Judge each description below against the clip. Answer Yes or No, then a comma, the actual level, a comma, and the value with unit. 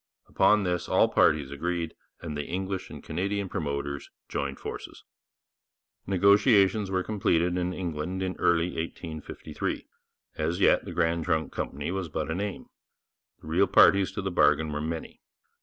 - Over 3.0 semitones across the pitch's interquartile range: Yes, average, 3.5 semitones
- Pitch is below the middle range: Yes, very low, 85 Hz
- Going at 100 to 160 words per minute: Yes, average, 150 wpm